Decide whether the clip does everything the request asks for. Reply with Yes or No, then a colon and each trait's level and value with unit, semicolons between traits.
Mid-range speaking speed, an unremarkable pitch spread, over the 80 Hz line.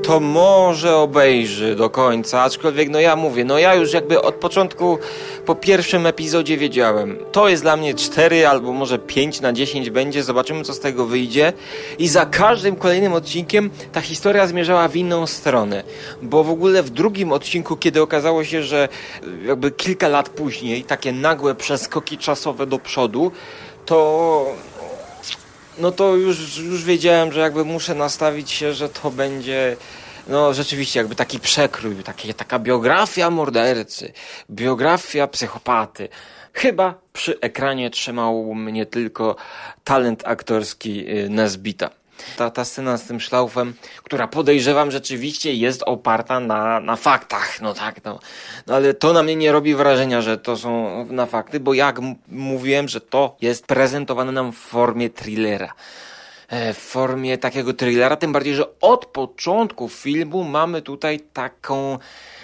Yes: average, 150 wpm; average, 4.4 semitones; medium, 140 Hz